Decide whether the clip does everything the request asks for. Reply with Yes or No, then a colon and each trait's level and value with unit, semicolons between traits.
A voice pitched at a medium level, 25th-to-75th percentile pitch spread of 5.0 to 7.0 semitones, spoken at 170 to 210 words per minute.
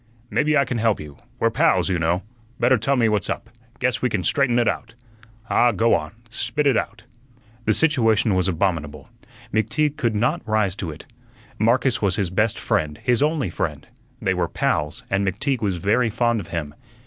No: low, 110 Hz; average, 5.3 semitones; average, 190 wpm